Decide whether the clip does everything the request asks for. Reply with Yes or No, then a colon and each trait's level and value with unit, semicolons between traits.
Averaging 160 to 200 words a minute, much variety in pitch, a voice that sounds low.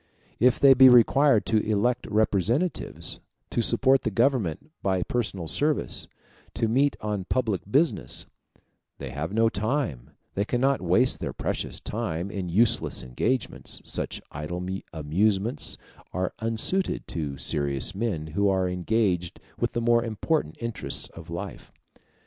No: slow, 135 wpm; wide, 5.7 semitones; low, 110 Hz